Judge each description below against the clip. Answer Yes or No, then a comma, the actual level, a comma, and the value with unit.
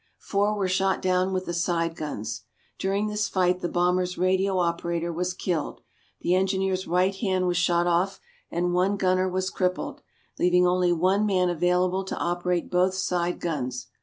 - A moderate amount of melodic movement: No, narrow, 1.3 semitones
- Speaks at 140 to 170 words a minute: Yes, average, 165 wpm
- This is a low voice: No, medium, 180 Hz